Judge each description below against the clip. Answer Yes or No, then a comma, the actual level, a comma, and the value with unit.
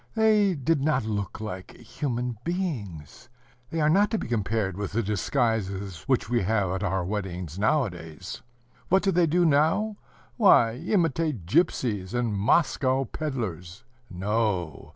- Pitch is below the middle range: Yes, low, 115 Hz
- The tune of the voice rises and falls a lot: Yes, wide, 8.0 semitones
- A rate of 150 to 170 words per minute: No, average, 140 wpm